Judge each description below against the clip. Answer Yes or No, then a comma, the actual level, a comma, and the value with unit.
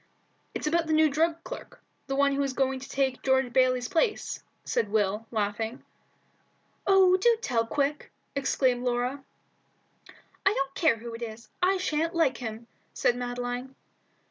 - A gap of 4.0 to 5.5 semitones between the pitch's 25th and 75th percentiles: Yes, average, 4.4 semitones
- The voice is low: No, very high, 265 Hz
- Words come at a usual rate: Yes, average, 155 wpm